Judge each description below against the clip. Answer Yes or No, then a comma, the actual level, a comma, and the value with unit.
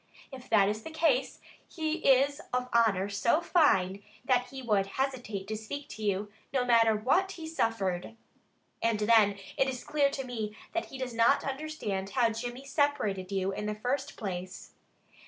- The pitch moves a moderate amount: Yes, average, 4.8 semitones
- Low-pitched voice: No, high, 235 Hz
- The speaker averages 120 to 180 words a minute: Yes, average, 175 wpm